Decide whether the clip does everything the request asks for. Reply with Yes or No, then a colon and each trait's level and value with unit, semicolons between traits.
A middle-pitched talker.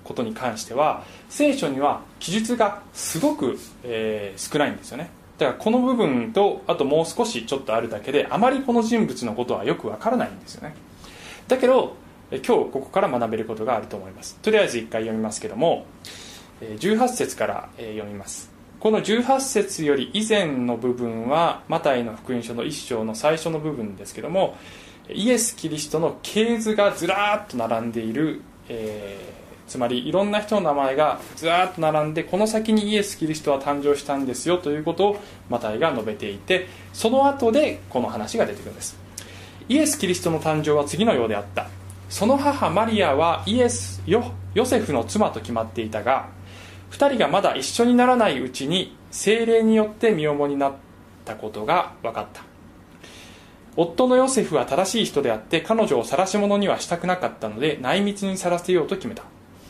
Yes: medium, 155 Hz